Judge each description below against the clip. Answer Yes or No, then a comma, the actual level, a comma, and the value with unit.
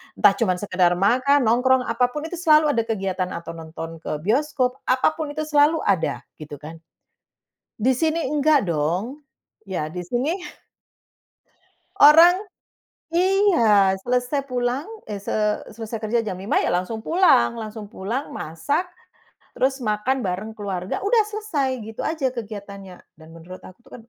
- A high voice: Yes, high, 235 Hz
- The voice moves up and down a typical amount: No, wide, 7.7 semitones